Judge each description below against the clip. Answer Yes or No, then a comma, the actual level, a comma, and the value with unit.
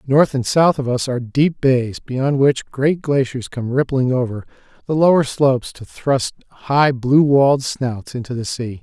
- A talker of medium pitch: No, low, 130 Hz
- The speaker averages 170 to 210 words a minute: Yes, average, 185 wpm